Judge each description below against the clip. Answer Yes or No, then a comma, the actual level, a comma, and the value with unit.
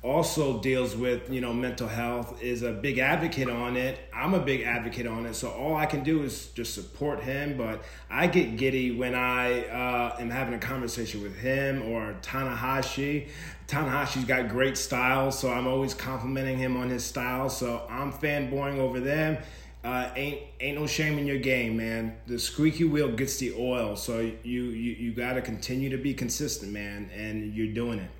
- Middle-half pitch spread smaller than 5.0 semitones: Yes, narrow, 2.5 semitones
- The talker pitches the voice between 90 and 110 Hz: No, low, 125 Hz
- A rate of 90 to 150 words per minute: No, average, 190 wpm